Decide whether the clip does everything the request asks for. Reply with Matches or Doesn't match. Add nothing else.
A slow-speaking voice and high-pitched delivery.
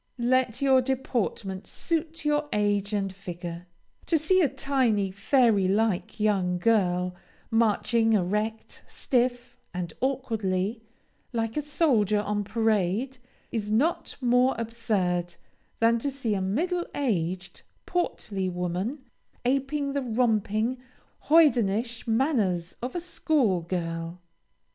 Matches